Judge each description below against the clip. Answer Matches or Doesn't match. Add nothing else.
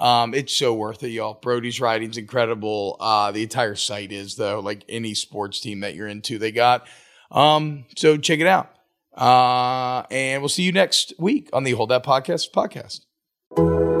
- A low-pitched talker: Matches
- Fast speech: Doesn't match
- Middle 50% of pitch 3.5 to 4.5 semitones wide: Matches